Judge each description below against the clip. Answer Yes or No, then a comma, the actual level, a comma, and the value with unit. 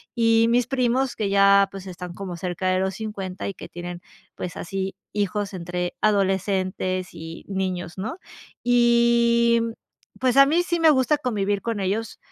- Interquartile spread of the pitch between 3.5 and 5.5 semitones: Yes, average, 4.1 semitones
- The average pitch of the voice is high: Yes, high, 200 Hz